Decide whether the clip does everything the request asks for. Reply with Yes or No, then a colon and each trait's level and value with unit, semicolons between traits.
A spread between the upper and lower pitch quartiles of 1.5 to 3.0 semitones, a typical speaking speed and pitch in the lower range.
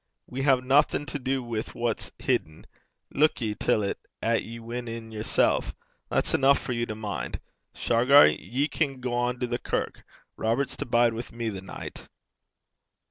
Yes: narrow, 2.6 semitones; average, 170 wpm; low, 120 Hz